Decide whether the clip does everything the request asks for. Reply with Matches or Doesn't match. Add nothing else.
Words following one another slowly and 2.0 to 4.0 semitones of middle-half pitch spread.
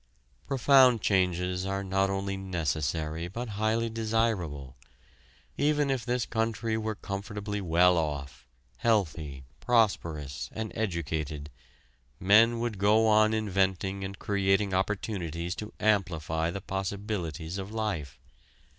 Doesn't match